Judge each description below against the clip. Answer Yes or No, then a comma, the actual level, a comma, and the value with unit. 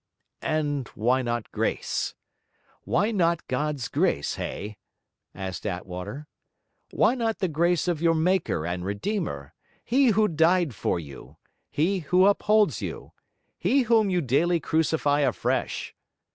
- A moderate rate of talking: No, slow, 130 wpm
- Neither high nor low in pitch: Yes, medium, 160 Hz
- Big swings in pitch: Yes, wide, 7.9 semitones